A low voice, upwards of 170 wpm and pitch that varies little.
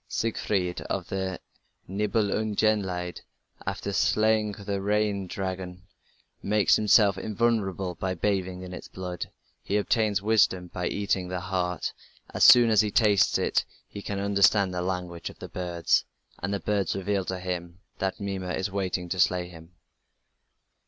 No: very low, 95 Hz; average, 145 wpm; narrow, 2.3 semitones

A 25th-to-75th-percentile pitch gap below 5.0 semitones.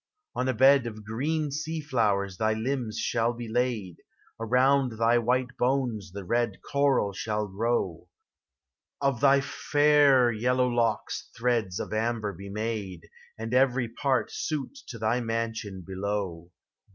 Yes: average, 3.4 semitones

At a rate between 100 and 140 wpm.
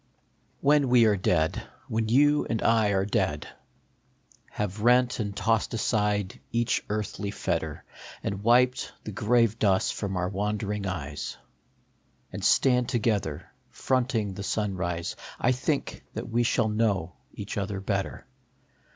Yes: slow, 135 wpm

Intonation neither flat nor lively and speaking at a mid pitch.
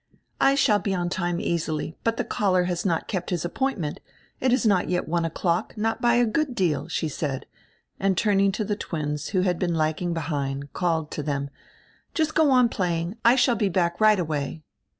Yes: average, 5.0 semitones; medium, 180 Hz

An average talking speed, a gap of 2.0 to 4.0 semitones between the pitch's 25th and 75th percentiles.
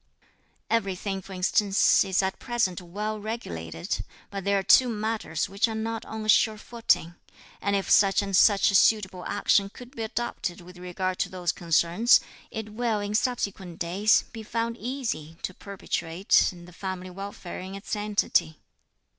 Yes: average, 160 wpm; average, 3.2 semitones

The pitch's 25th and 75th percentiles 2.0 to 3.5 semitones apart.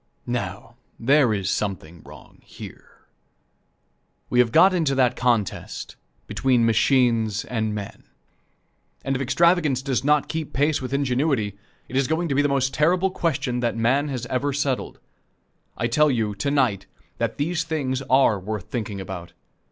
No: average, 4.4 semitones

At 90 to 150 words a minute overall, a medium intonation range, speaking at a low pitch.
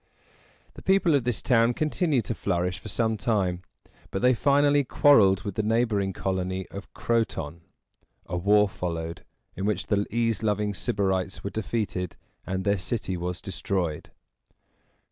Yes: average, 145 wpm; average, 3.8 semitones; low, 100 Hz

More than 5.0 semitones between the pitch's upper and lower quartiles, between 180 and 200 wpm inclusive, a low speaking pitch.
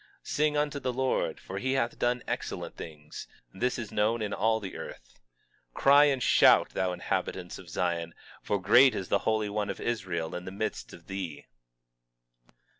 Yes: wide, 5.4 semitones; average, 190 wpm; low, 105 Hz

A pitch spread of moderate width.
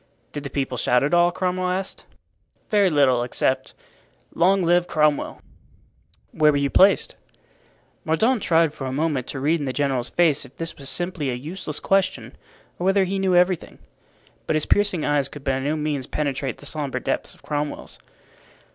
Yes: average, 4.4 semitones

